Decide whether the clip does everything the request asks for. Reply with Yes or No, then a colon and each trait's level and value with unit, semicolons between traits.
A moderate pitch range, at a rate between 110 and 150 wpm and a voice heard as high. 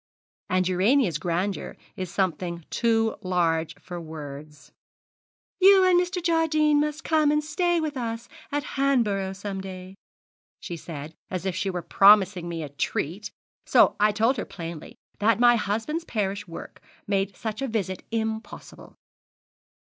No: wide, 7.2 semitones; average, 145 wpm; high, 205 Hz